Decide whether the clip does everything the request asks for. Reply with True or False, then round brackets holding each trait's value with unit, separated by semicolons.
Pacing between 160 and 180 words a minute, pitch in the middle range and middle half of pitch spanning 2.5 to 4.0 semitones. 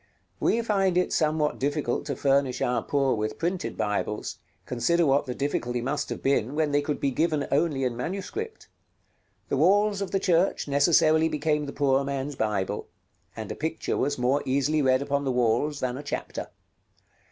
True (175 wpm; 145 Hz; 3.4 semitones)